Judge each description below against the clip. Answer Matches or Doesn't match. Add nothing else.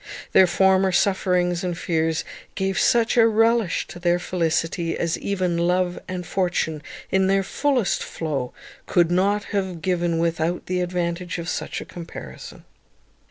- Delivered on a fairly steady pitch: Matches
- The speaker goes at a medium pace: Matches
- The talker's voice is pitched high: Doesn't match